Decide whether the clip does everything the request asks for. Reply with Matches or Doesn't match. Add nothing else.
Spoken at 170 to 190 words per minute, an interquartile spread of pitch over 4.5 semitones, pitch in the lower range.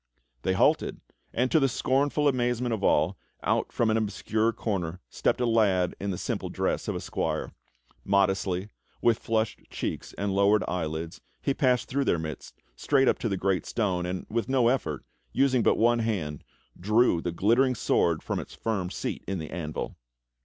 Matches